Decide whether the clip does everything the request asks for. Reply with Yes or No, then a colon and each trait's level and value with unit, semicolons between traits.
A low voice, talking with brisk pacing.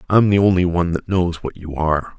Yes: very low, 90 Hz; fast, 245 wpm